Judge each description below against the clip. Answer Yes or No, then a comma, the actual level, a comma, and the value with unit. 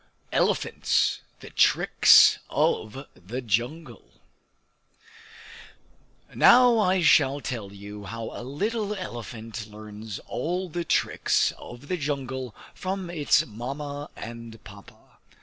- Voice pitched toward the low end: Yes, low, 130 Hz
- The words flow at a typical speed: No, slow, 105 wpm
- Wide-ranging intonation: Yes, wide, 7.0 semitones